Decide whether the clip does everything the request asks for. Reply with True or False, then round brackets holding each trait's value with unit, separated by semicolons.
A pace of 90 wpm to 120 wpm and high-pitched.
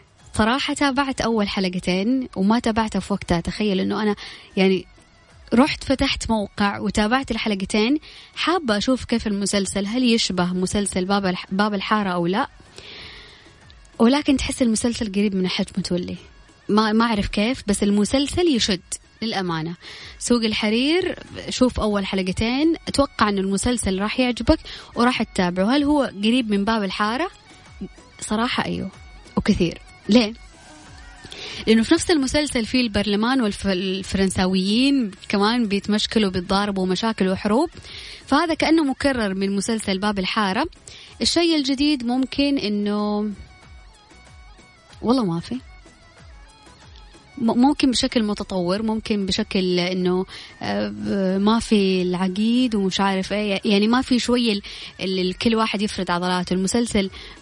True (115 wpm; 215 Hz)